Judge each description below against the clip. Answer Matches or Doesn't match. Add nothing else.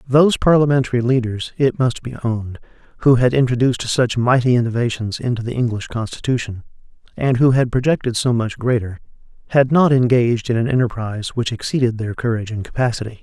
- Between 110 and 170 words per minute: Matches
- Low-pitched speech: Matches